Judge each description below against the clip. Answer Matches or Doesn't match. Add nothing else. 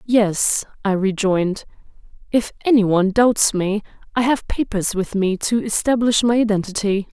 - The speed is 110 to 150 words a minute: Matches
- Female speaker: Matches